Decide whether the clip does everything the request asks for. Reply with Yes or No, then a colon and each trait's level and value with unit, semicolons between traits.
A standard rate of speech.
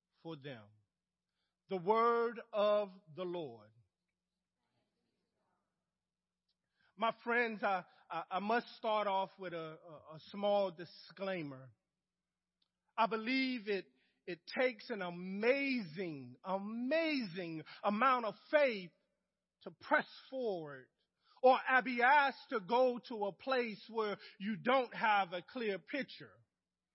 No: slow, 105 wpm